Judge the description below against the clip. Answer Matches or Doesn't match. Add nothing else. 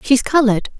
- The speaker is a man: Doesn't match